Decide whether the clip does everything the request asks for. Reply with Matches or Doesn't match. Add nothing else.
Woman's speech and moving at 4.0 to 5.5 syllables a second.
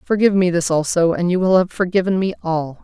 Doesn't match